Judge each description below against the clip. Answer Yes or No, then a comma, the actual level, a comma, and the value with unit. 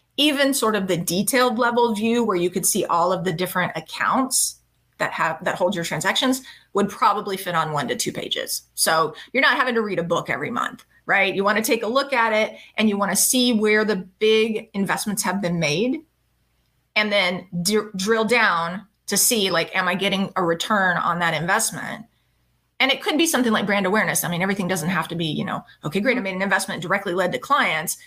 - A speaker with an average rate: No, fast, 225 wpm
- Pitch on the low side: No, high, 200 Hz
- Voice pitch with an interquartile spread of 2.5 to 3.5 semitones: No, average, 4.0 semitones